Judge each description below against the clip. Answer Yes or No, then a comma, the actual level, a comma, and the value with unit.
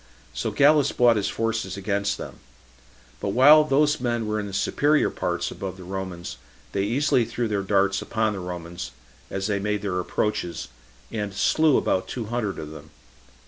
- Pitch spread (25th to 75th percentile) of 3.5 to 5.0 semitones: Yes, average, 3.8 semitones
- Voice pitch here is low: Yes, low, 105 Hz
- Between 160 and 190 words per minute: Yes, average, 175 wpm